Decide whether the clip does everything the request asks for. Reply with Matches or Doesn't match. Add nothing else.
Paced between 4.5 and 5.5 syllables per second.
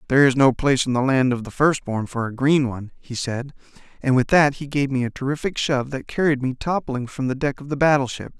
Doesn't match